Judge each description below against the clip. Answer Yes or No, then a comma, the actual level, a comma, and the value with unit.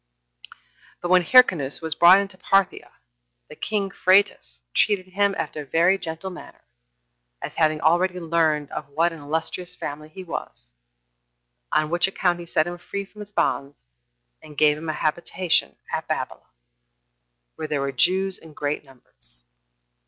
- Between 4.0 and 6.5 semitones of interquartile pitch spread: No, average, 3.6 semitones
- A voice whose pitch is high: No, medium, 165 Hz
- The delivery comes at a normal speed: Yes, average, 160 wpm